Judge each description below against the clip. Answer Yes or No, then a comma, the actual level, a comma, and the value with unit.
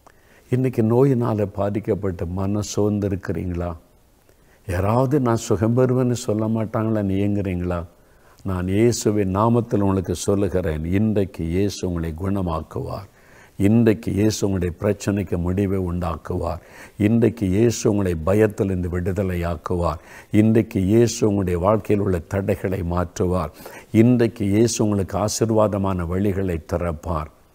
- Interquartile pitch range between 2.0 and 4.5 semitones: Yes, average, 3.3 semitones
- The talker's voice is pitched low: Yes, low, 100 Hz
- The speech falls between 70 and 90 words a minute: No, average, 100 wpm